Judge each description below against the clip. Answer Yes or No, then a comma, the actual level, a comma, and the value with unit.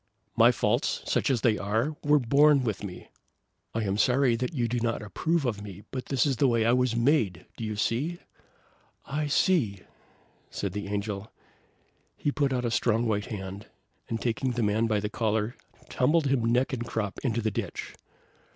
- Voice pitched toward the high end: No, low, 115 Hz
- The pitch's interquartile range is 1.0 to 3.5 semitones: No, average, 4.1 semitones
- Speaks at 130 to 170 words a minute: No, average, 190 wpm